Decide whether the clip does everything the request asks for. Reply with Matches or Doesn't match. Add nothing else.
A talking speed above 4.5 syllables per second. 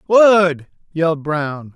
Doesn't match